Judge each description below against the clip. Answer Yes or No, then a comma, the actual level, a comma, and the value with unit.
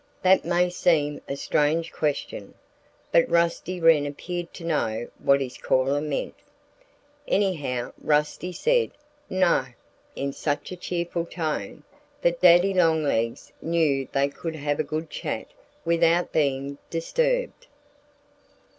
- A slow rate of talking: Yes, slow, 120 wpm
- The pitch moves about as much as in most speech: Yes, average, 3.5 semitones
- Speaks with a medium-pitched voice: Yes, medium, 165 Hz